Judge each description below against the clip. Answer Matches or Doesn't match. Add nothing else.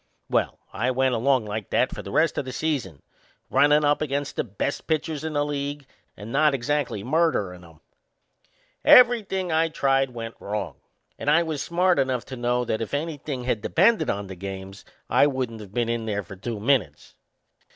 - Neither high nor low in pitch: Doesn't match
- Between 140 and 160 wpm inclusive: Doesn't match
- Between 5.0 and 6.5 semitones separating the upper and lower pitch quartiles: Matches